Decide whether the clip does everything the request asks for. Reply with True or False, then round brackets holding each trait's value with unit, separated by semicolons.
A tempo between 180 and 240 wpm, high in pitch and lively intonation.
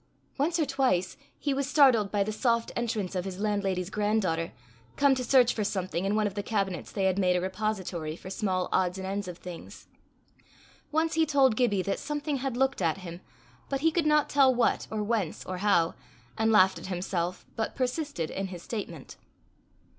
True (200 wpm; 210 Hz; 5.9 semitones)